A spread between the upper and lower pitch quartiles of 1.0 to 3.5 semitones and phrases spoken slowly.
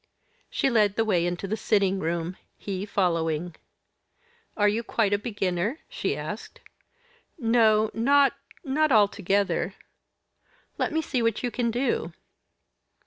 No: average, 3.9 semitones; slow, 130 wpm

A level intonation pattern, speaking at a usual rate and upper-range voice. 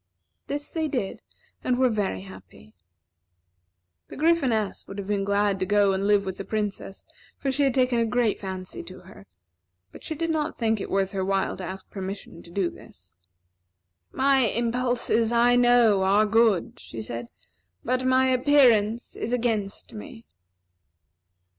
No: average, 4.3 semitones; average, 160 wpm; high, 215 Hz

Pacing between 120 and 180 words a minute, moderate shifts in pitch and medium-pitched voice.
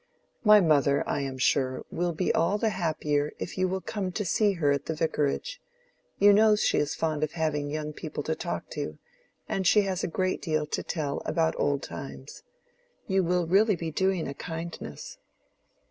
No: average, 190 wpm; average, 4.4 semitones; medium, 165 Hz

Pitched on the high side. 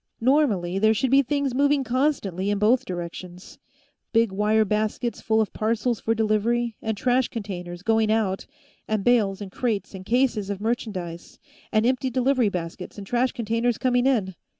Yes: high, 220 Hz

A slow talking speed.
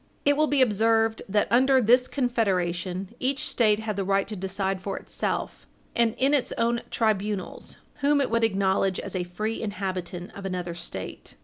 No: average, 175 wpm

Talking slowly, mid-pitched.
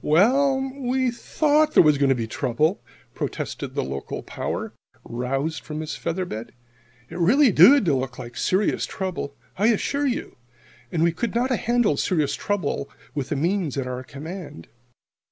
No: average, 165 wpm; medium, 170 Hz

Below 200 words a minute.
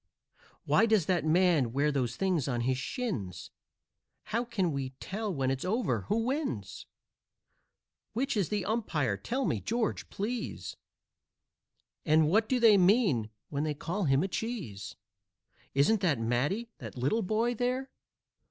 Yes: average, 145 wpm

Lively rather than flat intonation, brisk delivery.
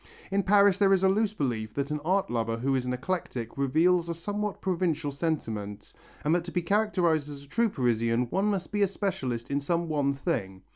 Yes: wide, 6.9 semitones; fast, 210 wpm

